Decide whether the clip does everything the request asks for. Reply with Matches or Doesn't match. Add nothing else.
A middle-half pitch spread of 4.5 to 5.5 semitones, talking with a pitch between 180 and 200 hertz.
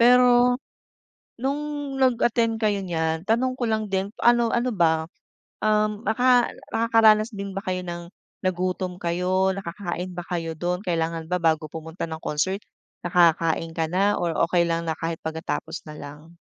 Matches